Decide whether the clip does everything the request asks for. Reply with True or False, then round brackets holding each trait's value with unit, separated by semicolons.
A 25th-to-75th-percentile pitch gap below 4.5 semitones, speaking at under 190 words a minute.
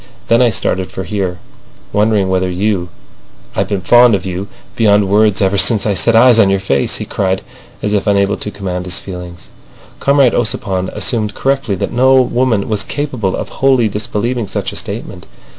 True (3.6 semitones; 175 wpm)